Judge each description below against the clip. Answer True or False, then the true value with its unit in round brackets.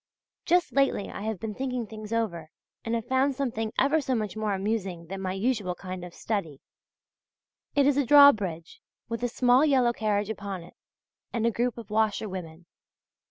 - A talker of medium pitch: False (220 Hz)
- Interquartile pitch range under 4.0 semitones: False (4.5 semitones)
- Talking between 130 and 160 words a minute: False (175 wpm)